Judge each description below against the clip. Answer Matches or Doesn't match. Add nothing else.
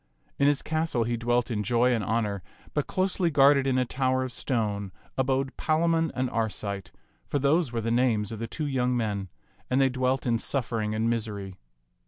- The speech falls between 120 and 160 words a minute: Doesn't match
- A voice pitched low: Matches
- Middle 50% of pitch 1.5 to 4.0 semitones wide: Matches